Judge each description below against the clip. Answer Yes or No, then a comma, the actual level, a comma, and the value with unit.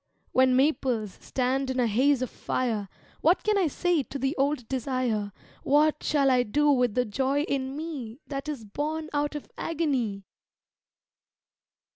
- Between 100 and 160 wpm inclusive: Yes, average, 155 wpm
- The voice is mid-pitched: No, very high, 270 Hz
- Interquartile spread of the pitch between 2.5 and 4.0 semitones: Yes, average, 3.0 semitones